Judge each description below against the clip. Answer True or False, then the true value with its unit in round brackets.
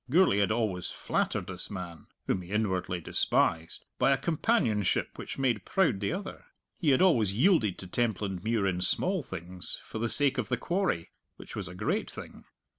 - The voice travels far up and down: True (6.8 semitones)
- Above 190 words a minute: False (180 wpm)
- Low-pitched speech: True (110 Hz)